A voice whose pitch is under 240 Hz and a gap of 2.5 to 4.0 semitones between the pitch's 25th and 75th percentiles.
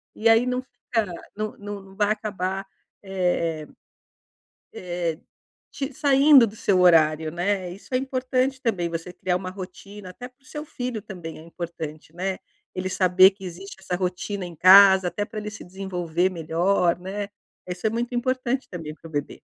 Yes: high, 190 Hz; average, 3.7 semitones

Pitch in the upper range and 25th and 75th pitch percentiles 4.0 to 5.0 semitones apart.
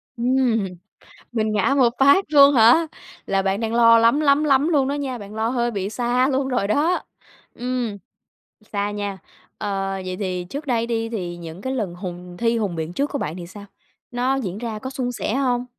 Yes: high, 230 Hz; average, 4.7 semitones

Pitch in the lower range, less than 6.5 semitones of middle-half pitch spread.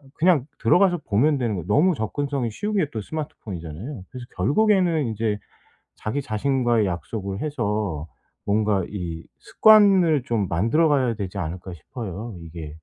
No: low, 115 Hz; wide, 7.0 semitones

